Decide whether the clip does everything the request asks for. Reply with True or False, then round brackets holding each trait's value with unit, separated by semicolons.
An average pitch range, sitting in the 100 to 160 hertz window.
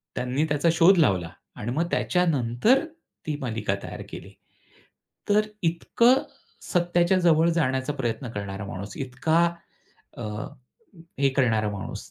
False (6.8 semitones; 140 Hz)